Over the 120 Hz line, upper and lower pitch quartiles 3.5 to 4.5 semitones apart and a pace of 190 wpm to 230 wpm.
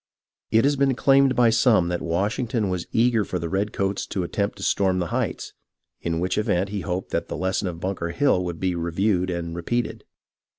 No: very low, 95 Hz; average, 4.2 semitones; average, 200 wpm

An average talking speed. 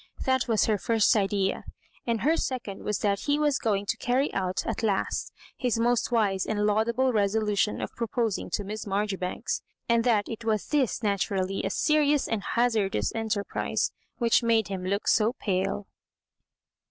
Yes: average, 165 wpm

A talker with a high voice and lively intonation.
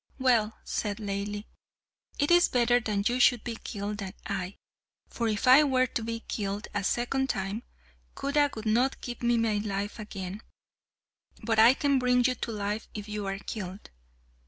No: high, 220 Hz; average, 3.3 semitones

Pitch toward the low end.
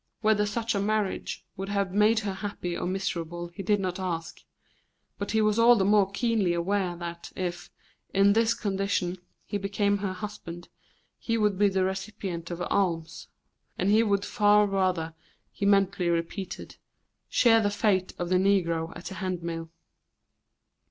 No: high, 195 Hz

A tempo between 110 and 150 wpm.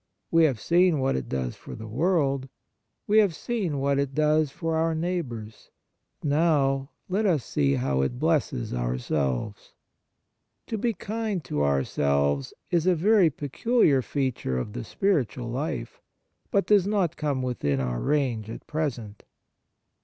Yes: average, 145 wpm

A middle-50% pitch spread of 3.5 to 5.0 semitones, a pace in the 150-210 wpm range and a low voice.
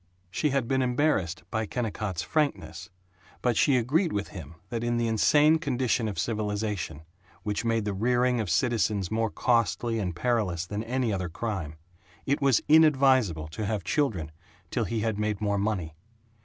Yes: average, 3.9 semitones; average, 165 wpm; low, 110 Hz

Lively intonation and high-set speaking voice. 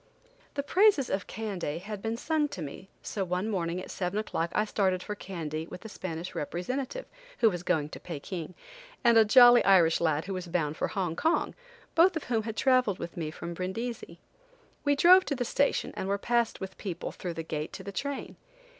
Yes: wide, 5.8 semitones; high, 195 Hz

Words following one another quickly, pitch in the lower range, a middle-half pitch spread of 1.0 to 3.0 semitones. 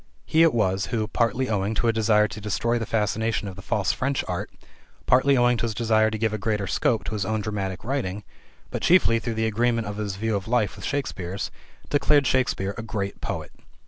Yes: fast, 215 wpm; low, 110 Hz; narrow, 2.6 semitones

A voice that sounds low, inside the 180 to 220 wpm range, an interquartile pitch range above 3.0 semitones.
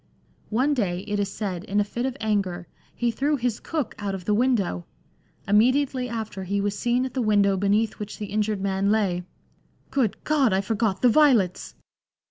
No: high, 210 Hz; average, 195 wpm; average, 3.7 semitones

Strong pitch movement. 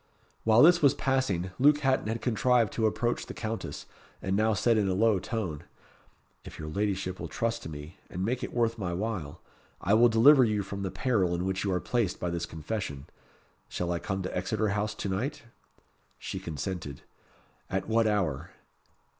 No: average, 4.1 semitones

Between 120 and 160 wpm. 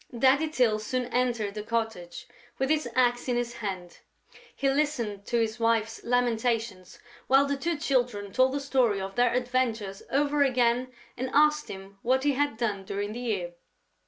No: average, 170 wpm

